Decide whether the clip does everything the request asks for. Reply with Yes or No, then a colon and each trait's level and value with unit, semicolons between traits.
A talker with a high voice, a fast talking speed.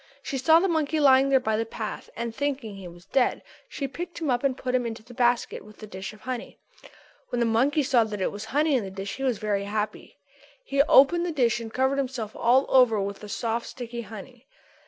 Yes: high, 245 Hz; fast, 240 wpm